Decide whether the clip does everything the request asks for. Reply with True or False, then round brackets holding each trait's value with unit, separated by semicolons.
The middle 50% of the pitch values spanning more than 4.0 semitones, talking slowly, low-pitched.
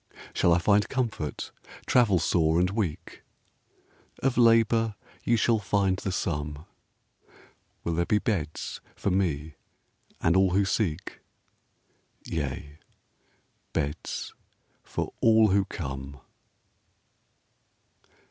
True (5.3 semitones; 100 wpm; 95 Hz)